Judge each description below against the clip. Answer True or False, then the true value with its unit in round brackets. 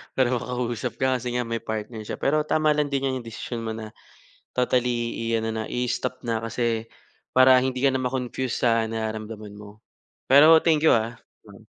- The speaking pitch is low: True (120 Hz)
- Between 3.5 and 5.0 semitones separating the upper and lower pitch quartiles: False (2.7 semitones)